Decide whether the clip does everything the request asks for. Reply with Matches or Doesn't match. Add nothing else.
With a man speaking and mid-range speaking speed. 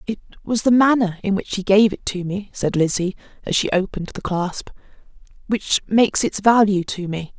Doesn't match